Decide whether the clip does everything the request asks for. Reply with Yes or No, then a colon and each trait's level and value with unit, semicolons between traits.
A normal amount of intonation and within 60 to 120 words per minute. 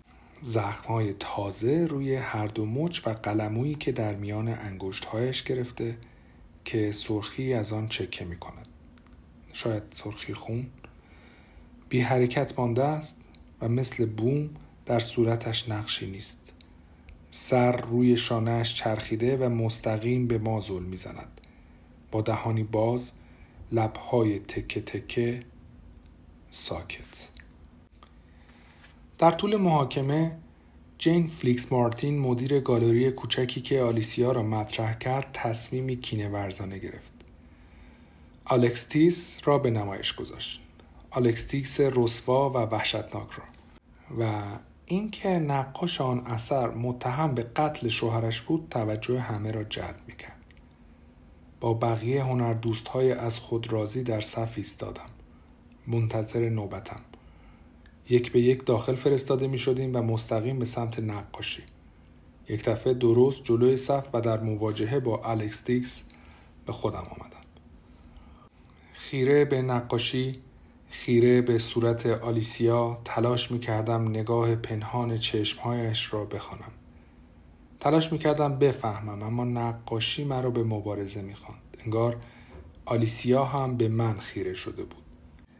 Yes: average, 4.1 semitones; average, 115 wpm